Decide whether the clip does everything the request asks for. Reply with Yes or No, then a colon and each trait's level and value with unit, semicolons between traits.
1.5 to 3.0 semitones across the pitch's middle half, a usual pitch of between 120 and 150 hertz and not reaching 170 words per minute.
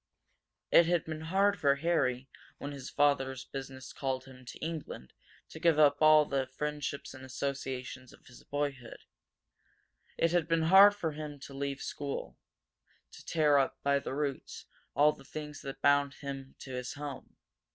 Yes: narrow, 2.4 semitones; medium, 140 Hz; average, 160 wpm